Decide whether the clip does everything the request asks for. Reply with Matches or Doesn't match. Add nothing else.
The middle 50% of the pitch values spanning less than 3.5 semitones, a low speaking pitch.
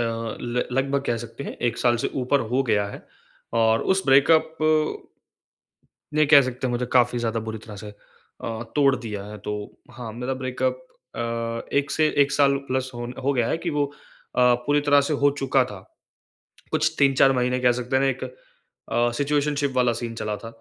Matches